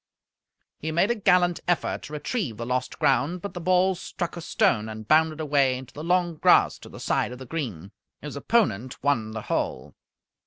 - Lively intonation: Yes, wide, 5.8 semitones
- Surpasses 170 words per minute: Yes, average, 195 wpm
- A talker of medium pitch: Yes, medium, 150 Hz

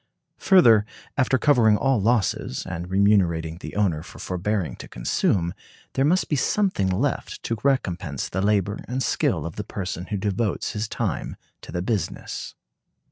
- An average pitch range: Yes, average, 4.8 semitones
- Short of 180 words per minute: Yes, average, 155 wpm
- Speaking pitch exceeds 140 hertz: No, low, 105 Hz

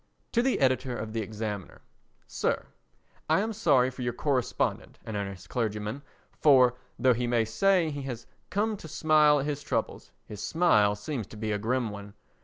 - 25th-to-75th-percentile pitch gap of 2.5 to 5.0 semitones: No, wide, 5.5 semitones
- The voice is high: No, low, 125 Hz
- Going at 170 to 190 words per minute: Yes, average, 180 wpm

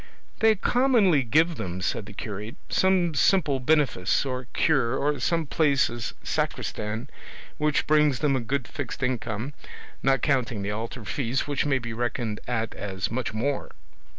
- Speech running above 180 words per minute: No, average, 155 wpm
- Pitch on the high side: No, low, 130 Hz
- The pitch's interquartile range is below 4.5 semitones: No, average, 4.9 semitones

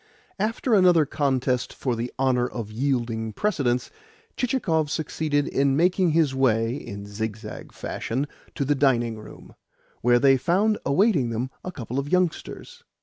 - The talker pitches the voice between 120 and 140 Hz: Yes, low, 135 Hz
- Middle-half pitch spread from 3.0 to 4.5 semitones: No, average, 5.3 semitones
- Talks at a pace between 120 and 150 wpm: Yes, average, 145 wpm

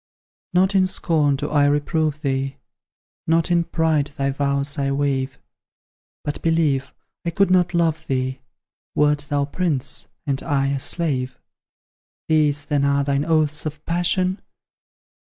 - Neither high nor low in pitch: Yes, medium, 145 Hz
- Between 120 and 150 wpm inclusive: Yes, average, 140 wpm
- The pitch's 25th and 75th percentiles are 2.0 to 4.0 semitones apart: Yes, average, 2.8 semitones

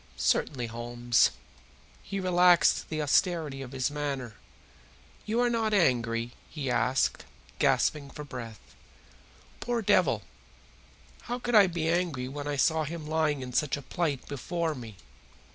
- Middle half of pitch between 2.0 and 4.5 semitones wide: No, average, 5.2 semitones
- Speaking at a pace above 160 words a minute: No, average, 140 wpm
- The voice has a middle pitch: Yes, medium, 145 Hz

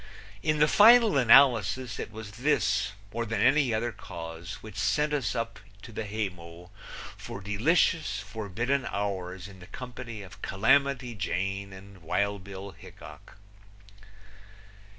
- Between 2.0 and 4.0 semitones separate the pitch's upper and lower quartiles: No, average, 4.7 semitones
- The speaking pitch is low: Yes, low, 110 Hz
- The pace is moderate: No, slow, 130 wpm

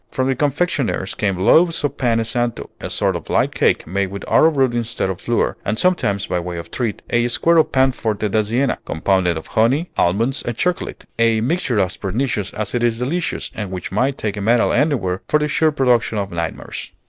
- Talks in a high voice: No, low, 115 Hz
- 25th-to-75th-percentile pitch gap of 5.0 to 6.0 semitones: Yes, average, 5.3 semitones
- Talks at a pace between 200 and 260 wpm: Yes, fast, 205 wpm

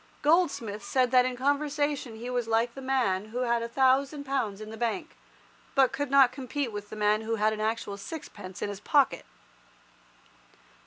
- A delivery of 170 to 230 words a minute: Yes, average, 180 wpm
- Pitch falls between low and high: No, high, 245 Hz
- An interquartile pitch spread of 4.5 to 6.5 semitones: No, average, 4.0 semitones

